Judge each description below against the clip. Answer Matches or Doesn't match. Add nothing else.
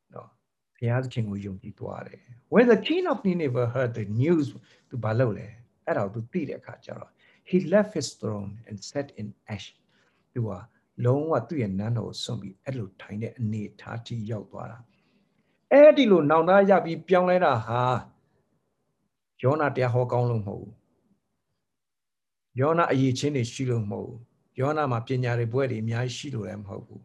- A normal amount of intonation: Matches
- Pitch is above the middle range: Doesn't match